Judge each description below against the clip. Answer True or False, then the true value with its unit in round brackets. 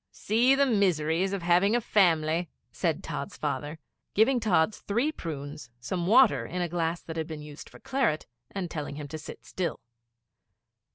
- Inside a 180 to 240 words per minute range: False (170 wpm)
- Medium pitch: True (175 Hz)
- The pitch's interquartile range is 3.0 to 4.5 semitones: False (5.1 semitones)